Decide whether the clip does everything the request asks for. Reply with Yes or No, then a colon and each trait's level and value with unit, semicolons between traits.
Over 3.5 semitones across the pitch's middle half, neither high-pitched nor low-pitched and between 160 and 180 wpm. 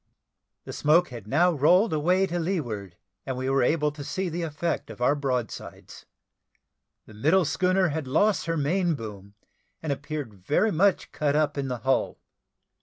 Yes: average, 5.0 semitones; medium, 150 Hz; average, 170 wpm